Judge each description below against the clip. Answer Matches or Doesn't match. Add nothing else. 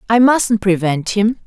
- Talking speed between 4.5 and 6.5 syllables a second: Doesn't match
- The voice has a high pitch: Matches